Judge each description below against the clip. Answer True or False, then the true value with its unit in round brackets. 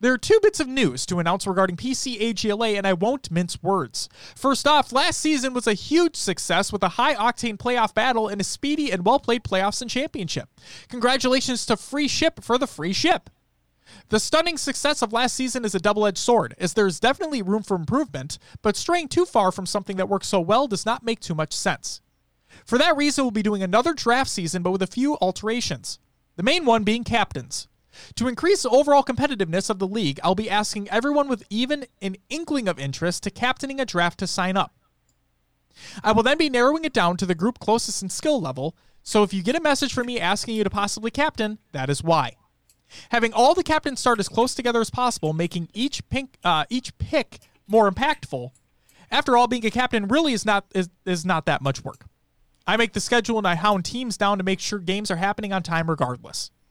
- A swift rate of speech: True (215 wpm)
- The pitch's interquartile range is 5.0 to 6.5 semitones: True (5.3 semitones)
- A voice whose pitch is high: True (220 Hz)